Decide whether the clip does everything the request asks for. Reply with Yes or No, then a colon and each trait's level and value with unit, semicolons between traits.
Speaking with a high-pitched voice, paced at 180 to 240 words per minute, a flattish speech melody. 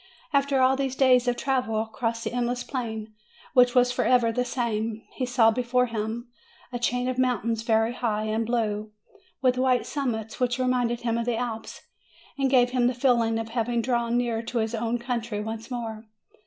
Yes: high, 240 Hz; average, 185 wpm; narrow, 1.8 semitones